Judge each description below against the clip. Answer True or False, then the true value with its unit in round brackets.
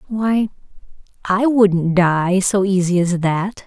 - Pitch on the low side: False (190 Hz)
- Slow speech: True (130 wpm)